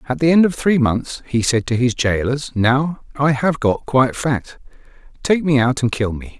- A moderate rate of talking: No, fast, 215 wpm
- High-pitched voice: No, low, 130 Hz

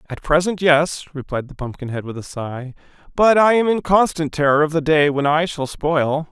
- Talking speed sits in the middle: No, fast, 210 wpm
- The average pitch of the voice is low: No, medium, 155 Hz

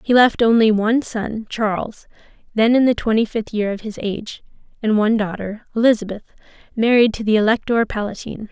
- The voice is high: Yes, high, 220 Hz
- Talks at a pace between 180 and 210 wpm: No, average, 170 wpm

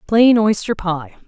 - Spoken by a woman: Yes, female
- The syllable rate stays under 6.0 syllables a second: Yes, 3.7 syllables/s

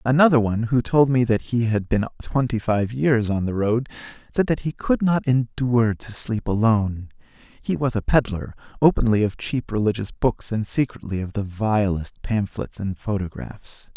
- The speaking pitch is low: Yes, low, 115 Hz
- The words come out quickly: No, average, 175 wpm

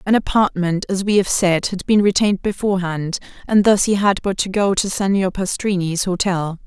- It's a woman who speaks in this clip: Yes, female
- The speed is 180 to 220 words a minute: Yes, average, 190 wpm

